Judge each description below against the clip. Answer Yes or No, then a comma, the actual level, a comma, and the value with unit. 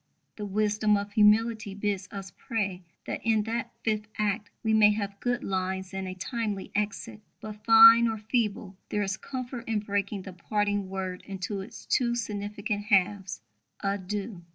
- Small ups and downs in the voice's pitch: Yes, narrow, 2.0 semitones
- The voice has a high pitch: Yes, high, 205 Hz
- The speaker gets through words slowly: No, average, 165 wpm